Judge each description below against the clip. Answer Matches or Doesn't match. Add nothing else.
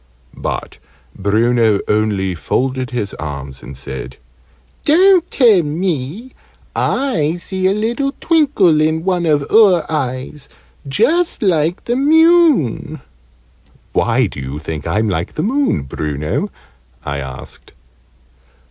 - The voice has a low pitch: Doesn't match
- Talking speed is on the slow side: Matches